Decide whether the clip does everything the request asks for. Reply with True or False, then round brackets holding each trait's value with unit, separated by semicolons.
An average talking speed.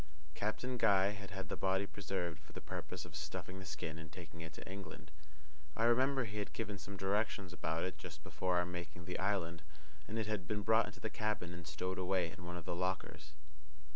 False (215 wpm)